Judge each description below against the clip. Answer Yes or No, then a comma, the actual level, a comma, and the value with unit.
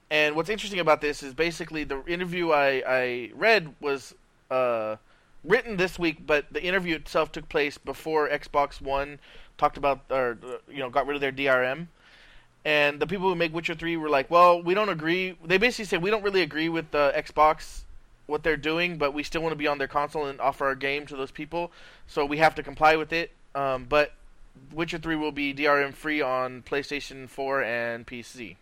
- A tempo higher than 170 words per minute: Yes, fast, 205 wpm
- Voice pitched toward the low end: No, medium, 150 Hz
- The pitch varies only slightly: No, average, 3.2 semitones